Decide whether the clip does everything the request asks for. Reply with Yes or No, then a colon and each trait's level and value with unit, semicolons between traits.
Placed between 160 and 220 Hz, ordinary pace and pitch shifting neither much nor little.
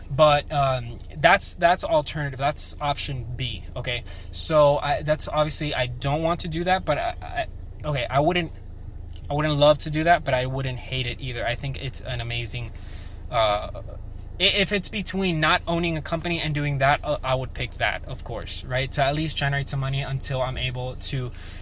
No: low, 135 Hz; average, 195 wpm; average, 4.2 semitones